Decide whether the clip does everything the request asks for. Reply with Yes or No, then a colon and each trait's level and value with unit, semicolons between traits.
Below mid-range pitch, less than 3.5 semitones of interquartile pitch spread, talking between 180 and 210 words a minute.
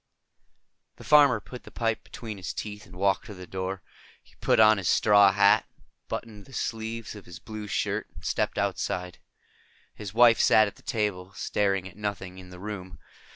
Yes: low, 105 Hz; average, 2.8 semitones; average, 185 wpm